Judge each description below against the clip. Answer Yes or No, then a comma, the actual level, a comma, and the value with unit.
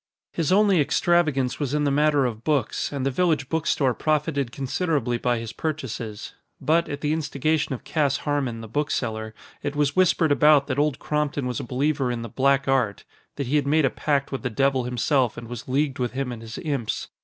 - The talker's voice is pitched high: No, medium, 140 Hz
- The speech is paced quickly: Yes, fast, 210 wpm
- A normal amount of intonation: Yes, average, 3.3 semitones